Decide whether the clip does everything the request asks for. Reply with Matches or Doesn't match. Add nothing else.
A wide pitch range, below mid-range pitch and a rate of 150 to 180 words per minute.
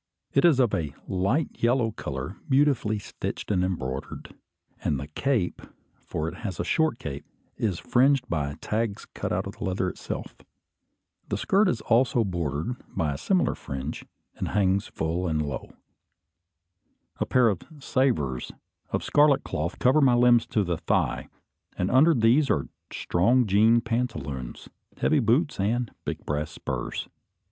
Matches